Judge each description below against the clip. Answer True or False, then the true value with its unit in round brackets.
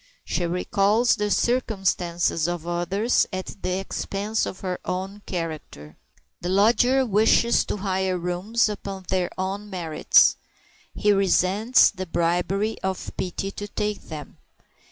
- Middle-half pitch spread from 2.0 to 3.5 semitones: True (2.7 semitones)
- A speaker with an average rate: False (130 wpm)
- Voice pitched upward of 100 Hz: True (190 Hz)